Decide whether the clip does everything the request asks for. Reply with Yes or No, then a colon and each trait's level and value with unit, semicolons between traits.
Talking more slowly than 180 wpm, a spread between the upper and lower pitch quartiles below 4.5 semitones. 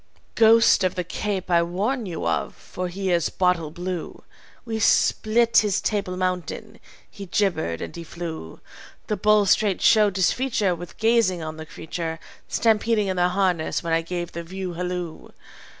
Yes: average, 165 wpm; average, 3.7 semitones